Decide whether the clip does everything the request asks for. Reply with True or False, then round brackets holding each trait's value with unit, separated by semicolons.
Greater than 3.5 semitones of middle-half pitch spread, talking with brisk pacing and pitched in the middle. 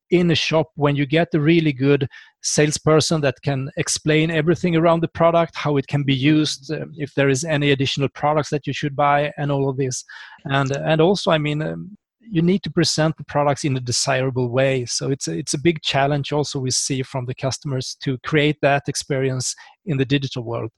False (2.6 semitones; 210 wpm; 145 Hz)